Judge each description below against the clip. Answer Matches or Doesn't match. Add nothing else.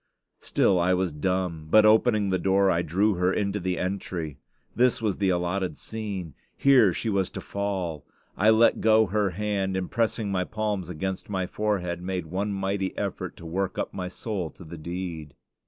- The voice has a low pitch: Matches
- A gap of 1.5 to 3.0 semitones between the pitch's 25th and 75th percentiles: Matches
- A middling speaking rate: Matches